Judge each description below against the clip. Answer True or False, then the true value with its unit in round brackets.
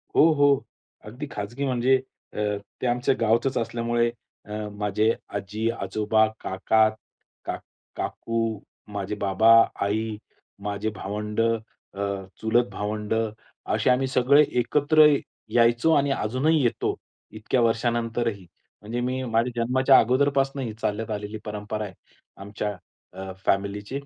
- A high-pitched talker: False (115 Hz)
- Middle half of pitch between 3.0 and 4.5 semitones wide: True (3.3 semitones)